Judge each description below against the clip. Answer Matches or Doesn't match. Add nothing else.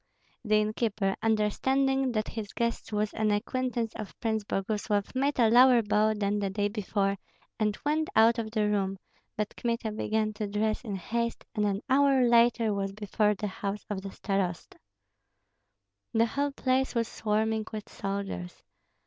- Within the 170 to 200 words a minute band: Doesn't match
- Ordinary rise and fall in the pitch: Doesn't match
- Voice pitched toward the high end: Matches